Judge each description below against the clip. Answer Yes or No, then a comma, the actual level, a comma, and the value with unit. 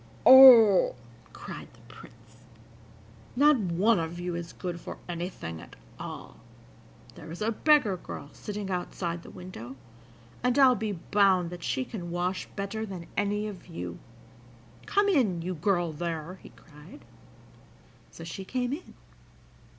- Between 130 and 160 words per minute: Yes, average, 145 wpm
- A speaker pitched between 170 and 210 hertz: Yes, medium, 185 Hz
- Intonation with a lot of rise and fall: No, average, 4.2 semitones